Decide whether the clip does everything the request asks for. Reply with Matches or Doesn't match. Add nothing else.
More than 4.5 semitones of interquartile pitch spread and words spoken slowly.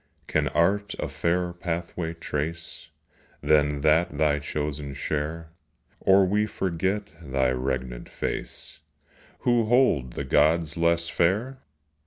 Doesn't match